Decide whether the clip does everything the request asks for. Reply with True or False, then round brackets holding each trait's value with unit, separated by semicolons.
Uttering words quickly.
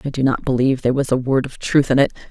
True (315 wpm)